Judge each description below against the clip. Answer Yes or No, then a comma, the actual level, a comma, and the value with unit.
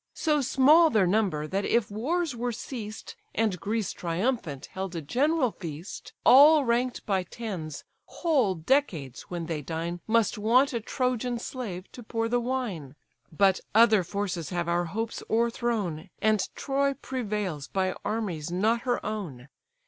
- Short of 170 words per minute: Yes, average, 150 wpm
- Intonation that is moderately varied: No, wide, 5.8 semitones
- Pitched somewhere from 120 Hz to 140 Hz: No, high, 215 Hz